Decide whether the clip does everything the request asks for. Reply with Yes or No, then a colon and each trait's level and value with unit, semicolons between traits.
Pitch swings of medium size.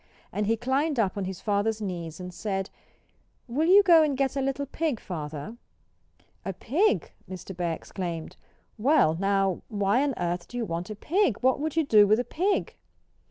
No: wide, 6.9 semitones